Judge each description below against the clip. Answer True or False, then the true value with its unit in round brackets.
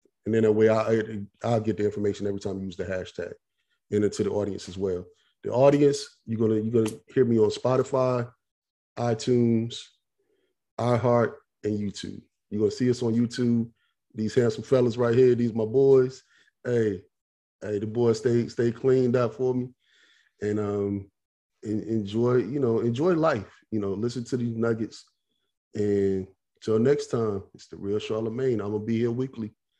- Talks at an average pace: True (175 wpm)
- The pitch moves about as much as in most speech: True (3.0 semitones)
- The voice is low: True (115 Hz)